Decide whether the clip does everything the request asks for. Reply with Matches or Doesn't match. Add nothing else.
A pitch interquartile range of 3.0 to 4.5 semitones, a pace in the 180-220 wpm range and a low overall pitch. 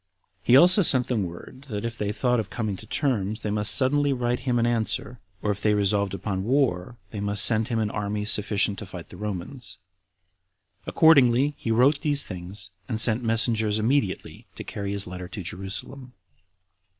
Matches